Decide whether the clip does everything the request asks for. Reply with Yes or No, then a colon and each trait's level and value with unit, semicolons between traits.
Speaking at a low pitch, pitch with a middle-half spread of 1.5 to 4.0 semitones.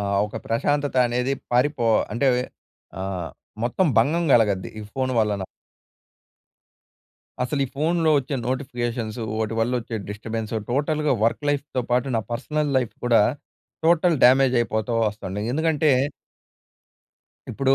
No: low, 125 Hz; average, 4.4 semitones